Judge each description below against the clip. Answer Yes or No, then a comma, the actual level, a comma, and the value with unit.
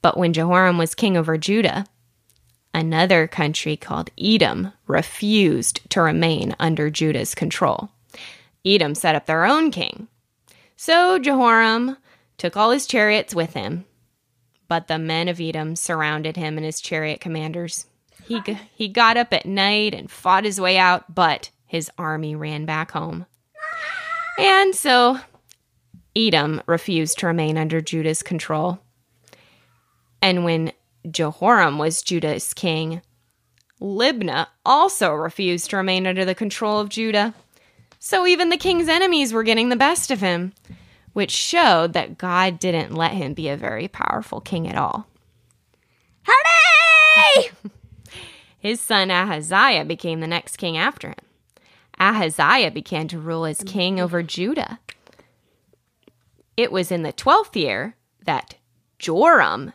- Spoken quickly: No, slow, 135 wpm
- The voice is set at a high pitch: No, medium, 175 Hz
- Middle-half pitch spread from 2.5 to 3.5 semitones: No, average, 5.3 semitones